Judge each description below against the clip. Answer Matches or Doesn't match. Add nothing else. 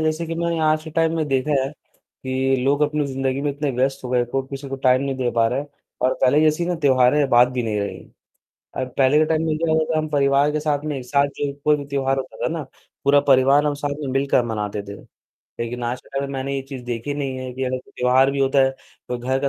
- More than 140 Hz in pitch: Doesn't match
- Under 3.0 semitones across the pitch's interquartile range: Matches